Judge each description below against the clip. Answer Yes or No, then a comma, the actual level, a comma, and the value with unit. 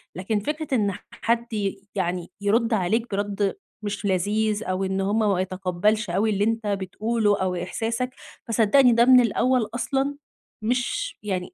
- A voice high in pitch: Yes, high, 210 Hz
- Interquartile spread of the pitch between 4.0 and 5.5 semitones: No, average, 3.3 semitones